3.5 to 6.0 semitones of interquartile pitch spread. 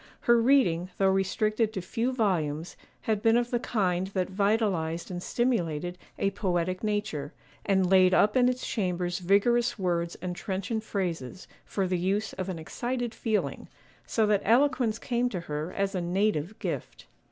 Yes: average, 3.9 semitones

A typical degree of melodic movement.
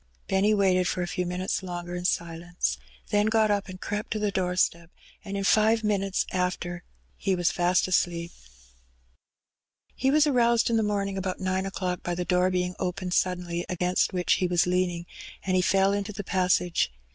No: narrow, 2.0 semitones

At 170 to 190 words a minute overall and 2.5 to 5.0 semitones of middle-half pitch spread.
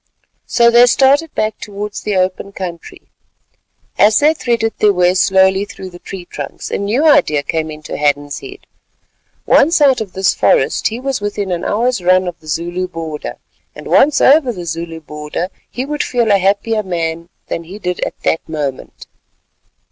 No: average, 175 wpm; wide, 5.6 semitones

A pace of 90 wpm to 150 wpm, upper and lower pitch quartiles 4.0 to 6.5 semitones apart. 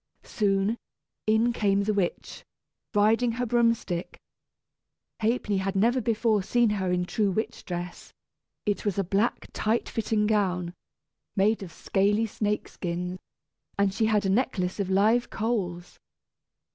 No: average, 145 wpm; average, 2.8 semitones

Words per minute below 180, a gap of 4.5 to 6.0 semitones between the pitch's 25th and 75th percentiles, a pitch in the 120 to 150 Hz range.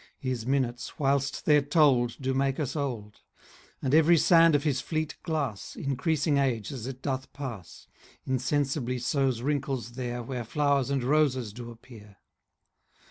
No: average, 150 wpm; average, 3.0 semitones; low, 135 Hz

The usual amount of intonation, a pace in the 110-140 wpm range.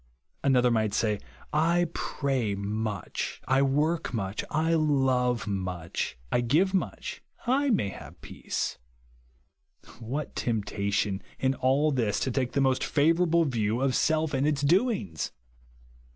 No: wide, 6.0 semitones; slow, 135 wpm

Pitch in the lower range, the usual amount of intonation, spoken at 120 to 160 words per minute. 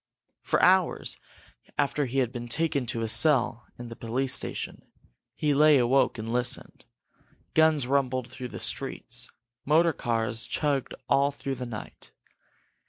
Yes: low, 130 Hz; average, 3.3 semitones; average, 150 wpm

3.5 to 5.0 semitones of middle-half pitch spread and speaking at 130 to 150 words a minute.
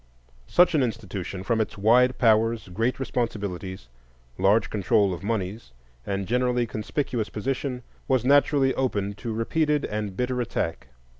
Yes: average, 4.0 semitones; slow, 135 wpm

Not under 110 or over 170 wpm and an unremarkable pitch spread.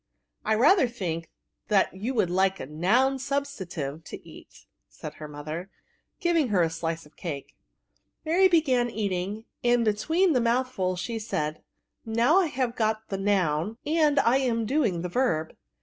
No: average, 165 wpm; wide, 7.0 semitones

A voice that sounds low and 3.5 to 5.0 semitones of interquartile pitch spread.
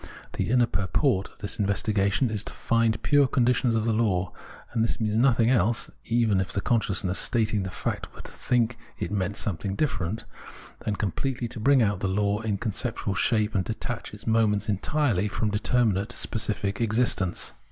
No: low, 110 Hz; average, 2.8 semitones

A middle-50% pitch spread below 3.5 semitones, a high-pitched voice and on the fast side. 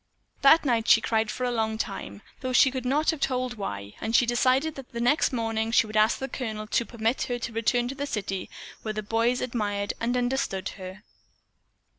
Yes: average, 2.9 semitones; high, 235 Hz; fast, 215 wpm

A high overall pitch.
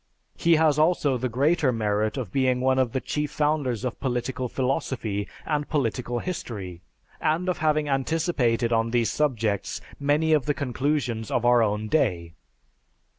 No: low, 130 Hz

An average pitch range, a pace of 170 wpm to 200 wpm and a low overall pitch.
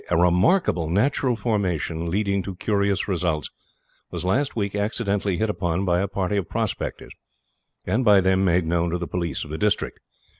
Yes: average, 3.0 semitones; average, 175 wpm; very low, 95 Hz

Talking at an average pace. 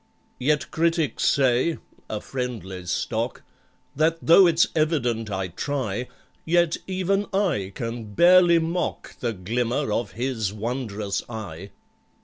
No: slow, 120 wpm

